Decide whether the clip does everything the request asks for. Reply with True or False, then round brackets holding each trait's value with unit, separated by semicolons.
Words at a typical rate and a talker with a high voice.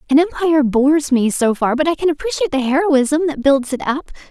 False (225 wpm; 290 Hz)